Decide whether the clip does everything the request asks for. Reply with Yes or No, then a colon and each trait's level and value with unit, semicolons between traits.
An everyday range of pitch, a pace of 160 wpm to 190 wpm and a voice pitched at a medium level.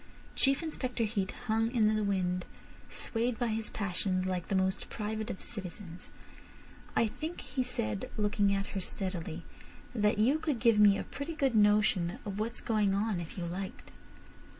No: average, 3.5 semitones; average, 170 wpm; high, 210 Hz